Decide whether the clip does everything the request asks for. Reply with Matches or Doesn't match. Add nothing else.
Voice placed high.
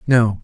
Doesn't match